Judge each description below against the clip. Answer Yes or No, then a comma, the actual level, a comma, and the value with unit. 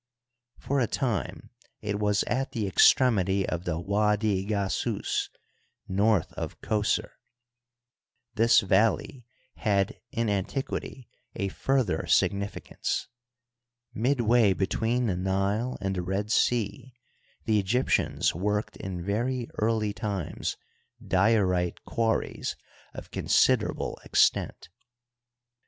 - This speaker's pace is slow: Yes, slow, 105 wpm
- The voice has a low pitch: Yes, low, 105 Hz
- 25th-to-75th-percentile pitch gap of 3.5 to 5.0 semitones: No, average, 3.1 semitones